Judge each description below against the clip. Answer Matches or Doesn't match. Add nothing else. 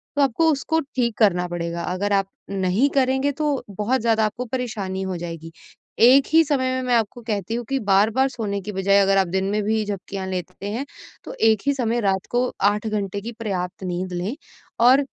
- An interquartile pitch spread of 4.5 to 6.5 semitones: Matches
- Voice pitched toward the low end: Doesn't match